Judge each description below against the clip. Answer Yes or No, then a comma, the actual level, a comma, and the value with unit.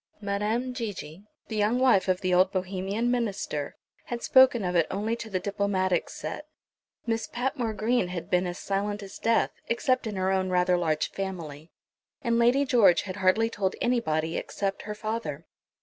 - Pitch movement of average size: Yes, average, 4.0 semitones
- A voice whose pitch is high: Yes, high, 200 Hz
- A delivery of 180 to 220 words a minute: No, average, 170 wpm